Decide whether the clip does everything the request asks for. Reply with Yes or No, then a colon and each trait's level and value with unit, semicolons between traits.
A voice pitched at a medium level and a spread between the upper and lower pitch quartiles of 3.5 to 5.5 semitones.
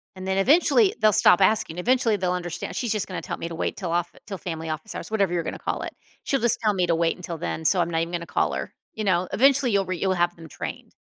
Yes: medium, 180 Hz; average, 3.9 semitones